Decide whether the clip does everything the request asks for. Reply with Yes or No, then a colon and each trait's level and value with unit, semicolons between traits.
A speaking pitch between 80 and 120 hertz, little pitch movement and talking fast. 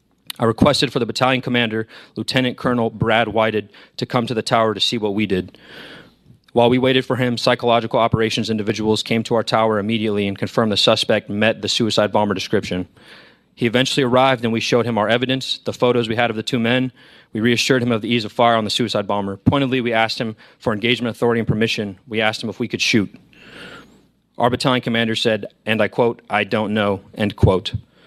Yes: low, 115 Hz; narrow, 2.2 semitones; fast, 210 wpm